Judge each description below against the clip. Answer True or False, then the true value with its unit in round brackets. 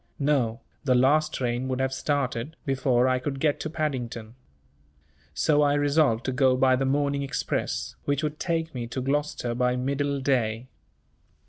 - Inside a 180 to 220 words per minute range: False (160 wpm)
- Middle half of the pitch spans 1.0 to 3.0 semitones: True (2.5 semitones)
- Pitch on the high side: False (135 Hz)